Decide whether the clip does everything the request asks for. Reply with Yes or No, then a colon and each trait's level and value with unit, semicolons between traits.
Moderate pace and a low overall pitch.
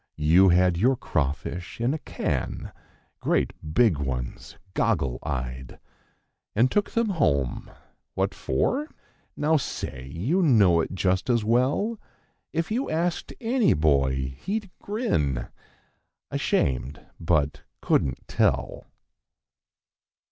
No: slow, 105 wpm; very low, 90 Hz